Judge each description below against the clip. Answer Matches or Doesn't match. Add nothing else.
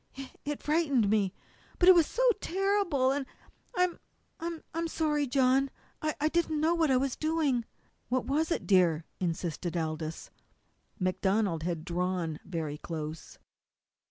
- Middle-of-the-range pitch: Doesn't match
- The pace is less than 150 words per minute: Matches